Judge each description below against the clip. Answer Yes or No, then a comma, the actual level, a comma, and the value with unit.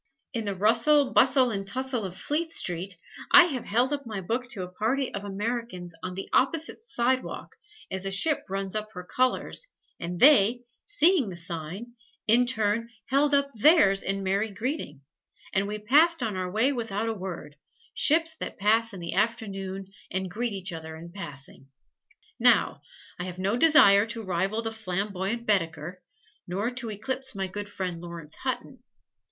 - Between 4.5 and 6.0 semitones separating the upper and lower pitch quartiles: Yes, average, 4.8 semitones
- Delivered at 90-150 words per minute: No, average, 170 wpm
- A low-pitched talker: No, high, 210 Hz